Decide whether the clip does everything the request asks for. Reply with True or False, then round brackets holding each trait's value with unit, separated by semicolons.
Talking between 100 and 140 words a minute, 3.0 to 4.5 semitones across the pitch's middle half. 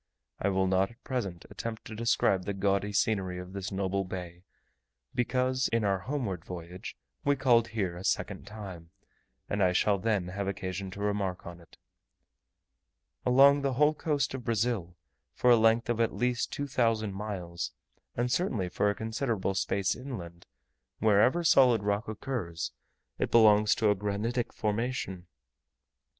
False (155 wpm; 4.0 semitones)